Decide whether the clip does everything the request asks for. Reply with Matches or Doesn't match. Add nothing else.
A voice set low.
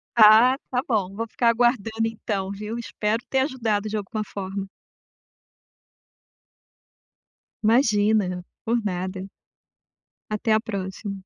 Doesn't match